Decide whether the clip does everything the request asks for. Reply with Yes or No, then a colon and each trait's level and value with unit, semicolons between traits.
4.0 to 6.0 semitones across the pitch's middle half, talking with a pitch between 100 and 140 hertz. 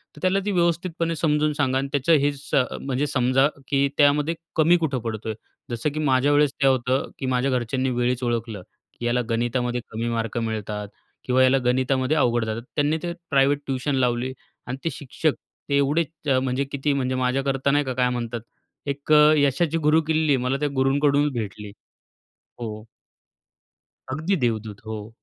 No: average, 3.3 semitones; low, 135 Hz